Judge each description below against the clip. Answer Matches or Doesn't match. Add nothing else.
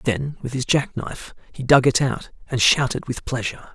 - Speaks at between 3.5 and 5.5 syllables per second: Matches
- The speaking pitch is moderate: Doesn't match